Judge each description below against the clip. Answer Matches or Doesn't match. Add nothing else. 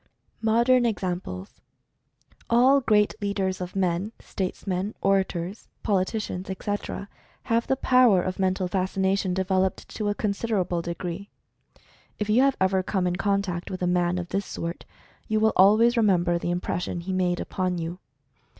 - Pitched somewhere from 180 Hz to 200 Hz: Matches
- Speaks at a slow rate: Doesn't match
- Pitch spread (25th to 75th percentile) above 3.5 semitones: Doesn't match